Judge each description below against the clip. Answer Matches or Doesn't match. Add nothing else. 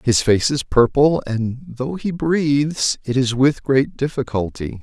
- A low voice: Matches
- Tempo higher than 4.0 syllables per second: Doesn't match